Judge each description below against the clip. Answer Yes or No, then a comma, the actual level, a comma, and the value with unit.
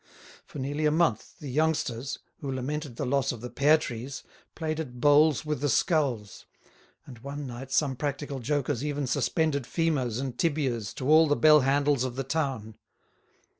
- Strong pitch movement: No, average, 3.0 semitones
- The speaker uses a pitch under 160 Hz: Yes, medium, 140 Hz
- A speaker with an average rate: Yes, average, 170 wpm